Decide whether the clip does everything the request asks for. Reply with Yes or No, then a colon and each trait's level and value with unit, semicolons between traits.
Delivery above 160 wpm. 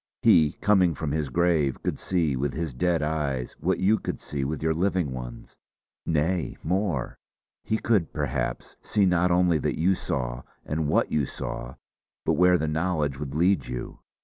Yes: average, 175 wpm